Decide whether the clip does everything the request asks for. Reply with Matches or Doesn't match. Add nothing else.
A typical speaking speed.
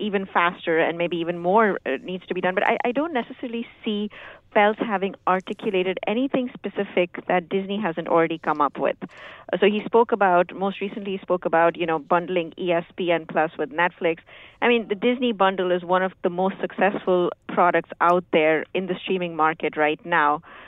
Matches